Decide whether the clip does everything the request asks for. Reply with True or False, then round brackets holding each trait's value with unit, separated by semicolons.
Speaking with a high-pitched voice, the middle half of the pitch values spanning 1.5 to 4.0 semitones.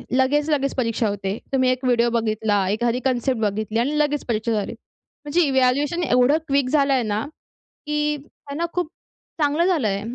False (255 Hz; 4.7 semitones)